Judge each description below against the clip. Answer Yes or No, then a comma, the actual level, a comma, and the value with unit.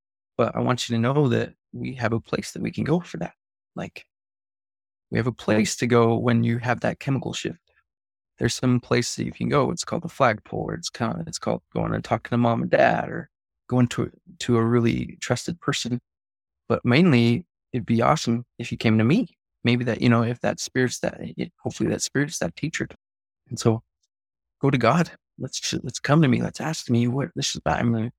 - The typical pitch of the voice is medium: No, low, 120 Hz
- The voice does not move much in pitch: Yes, narrow, 2.0 semitones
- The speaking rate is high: Yes, fast, 215 wpm